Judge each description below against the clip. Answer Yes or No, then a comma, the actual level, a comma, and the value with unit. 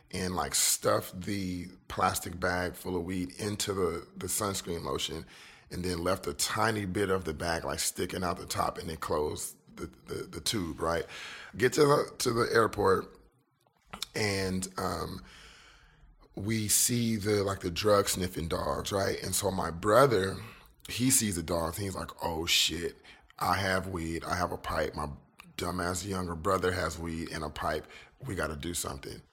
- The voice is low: Yes, very low, 95 Hz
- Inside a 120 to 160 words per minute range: No, average, 175 wpm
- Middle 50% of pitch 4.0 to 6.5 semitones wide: No, average, 2.8 semitones